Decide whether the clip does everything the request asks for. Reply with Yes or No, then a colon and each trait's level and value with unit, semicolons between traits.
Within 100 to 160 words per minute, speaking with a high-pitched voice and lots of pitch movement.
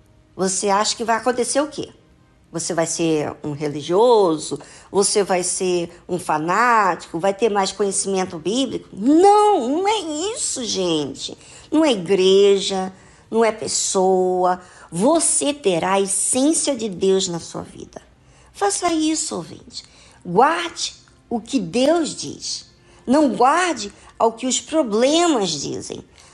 Yes: average, 130 wpm; high, 210 Hz; wide, 8.2 semitones